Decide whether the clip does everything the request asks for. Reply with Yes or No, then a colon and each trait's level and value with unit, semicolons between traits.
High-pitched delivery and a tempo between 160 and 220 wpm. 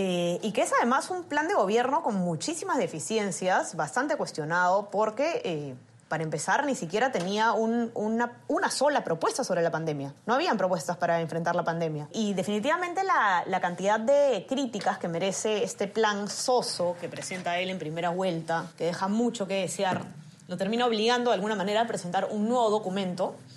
Yes: high, 195 Hz; average, 180 wpm